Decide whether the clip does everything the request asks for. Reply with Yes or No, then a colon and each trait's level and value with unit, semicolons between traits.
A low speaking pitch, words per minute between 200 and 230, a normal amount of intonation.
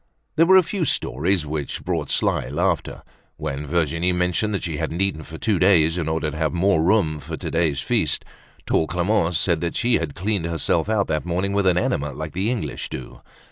Yes: very low, 85 Hz; fast, 205 wpm; average, 3.9 semitones